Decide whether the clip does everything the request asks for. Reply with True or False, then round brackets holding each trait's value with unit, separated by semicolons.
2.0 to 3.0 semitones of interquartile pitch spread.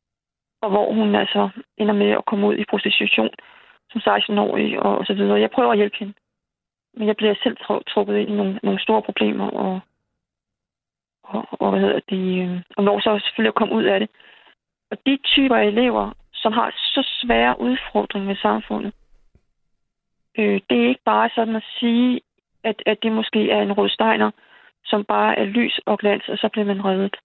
True (2.4 semitones)